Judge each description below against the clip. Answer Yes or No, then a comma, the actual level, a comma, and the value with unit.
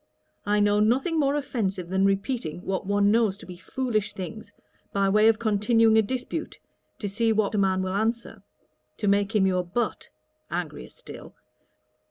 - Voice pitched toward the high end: Yes, high, 210 Hz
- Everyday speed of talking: Yes, average, 170 wpm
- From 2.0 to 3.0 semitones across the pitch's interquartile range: Yes, average, 2.7 semitones